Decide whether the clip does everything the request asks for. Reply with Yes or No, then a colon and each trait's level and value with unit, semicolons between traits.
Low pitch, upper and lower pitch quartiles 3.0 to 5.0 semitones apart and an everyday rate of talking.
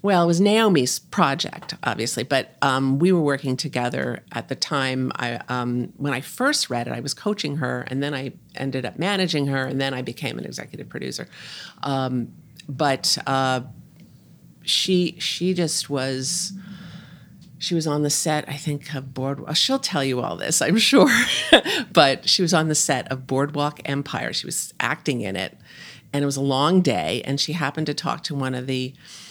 No: medium, 145 Hz; average, 4.2 semitones; average, 190 wpm